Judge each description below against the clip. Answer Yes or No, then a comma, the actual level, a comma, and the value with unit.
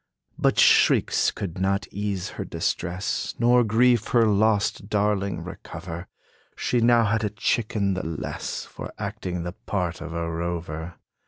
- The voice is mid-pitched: No, low, 100 Hz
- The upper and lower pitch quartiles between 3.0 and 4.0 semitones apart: Yes, average, 3.7 semitones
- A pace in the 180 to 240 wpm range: No, average, 145 wpm